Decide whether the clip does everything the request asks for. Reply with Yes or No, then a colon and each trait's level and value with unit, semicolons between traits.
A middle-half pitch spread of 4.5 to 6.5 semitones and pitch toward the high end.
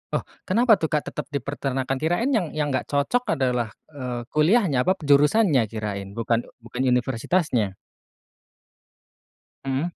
No: average, 5.3 semitones; medium, 140 Hz